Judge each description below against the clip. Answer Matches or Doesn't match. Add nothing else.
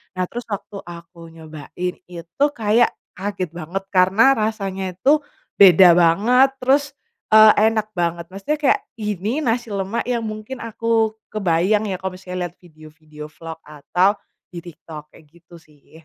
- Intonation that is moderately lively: Matches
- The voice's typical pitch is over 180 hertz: Matches